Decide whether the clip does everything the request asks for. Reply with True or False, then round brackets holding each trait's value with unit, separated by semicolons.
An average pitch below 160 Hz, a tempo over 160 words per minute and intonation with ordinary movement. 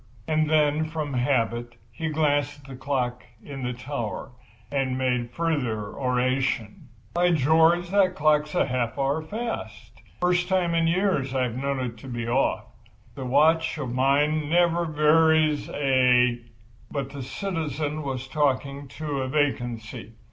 False (140 Hz; 145 wpm; 3.7 semitones)